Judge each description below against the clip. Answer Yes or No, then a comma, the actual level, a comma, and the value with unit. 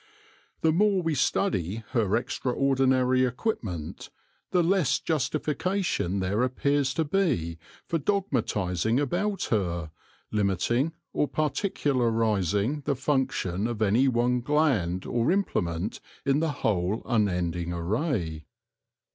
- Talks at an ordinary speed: No, slow, 105 wpm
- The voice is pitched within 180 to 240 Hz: No, low, 125 Hz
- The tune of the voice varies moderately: No, wide, 7.4 semitones